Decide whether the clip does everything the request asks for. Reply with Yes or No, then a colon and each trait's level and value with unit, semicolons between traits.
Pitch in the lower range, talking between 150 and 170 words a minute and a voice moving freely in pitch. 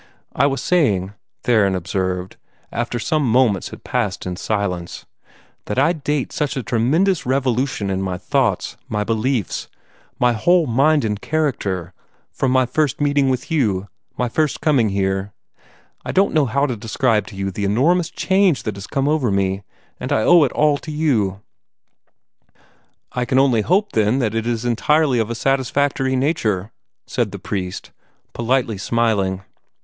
Yes: low, 120 Hz; average, 160 wpm; wide, 5.7 semitones